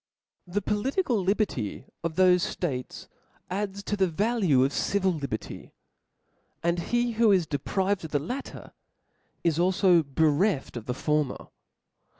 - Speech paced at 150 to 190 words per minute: No, slow, 135 wpm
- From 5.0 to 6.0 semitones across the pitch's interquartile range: Yes, average, 5.3 semitones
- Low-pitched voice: No, medium, 180 Hz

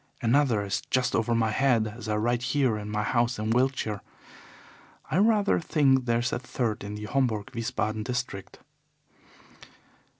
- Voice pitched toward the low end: Yes, low, 120 Hz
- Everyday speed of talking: Yes, average, 160 wpm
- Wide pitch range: No, average, 3.2 semitones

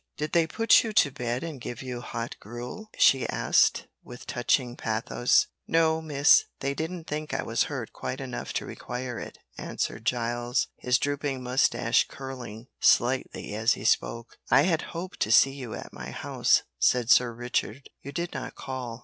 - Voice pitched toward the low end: Yes, low, 130 Hz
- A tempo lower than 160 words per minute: No, average, 175 wpm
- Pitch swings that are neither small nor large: Yes, average, 3.8 semitones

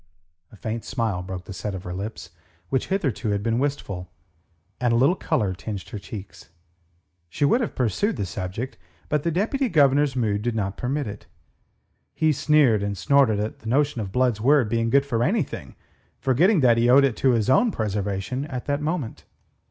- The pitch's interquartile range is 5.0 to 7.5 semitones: Yes, wide, 5.5 semitones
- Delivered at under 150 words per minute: No, average, 190 wpm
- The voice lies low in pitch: Yes, low, 120 Hz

